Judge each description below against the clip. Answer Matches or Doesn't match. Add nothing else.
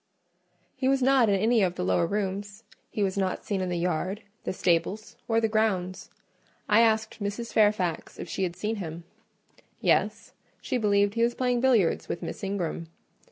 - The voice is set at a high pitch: Matches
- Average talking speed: Matches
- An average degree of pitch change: Matches